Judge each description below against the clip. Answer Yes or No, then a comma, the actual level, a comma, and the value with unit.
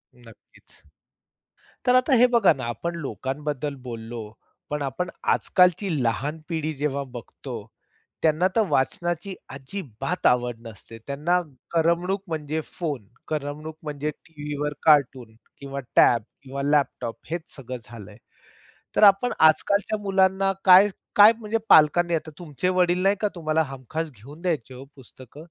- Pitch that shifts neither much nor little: Yes, average, 5.0 semitones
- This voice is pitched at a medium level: Yes, medium, 150 Hz